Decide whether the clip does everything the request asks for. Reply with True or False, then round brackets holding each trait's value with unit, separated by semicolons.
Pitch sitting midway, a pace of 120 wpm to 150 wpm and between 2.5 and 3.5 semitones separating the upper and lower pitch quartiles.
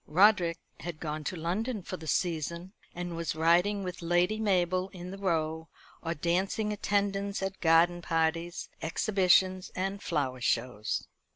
True (175 Hz; 145 wpm; 2.9 semitones)